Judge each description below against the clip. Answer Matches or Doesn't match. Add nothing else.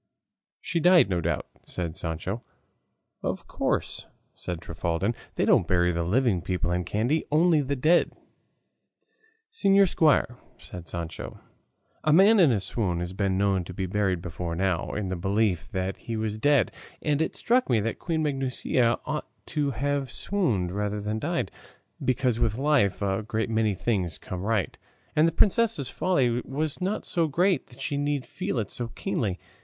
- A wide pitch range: Matches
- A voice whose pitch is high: Doesn't match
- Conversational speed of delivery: Matches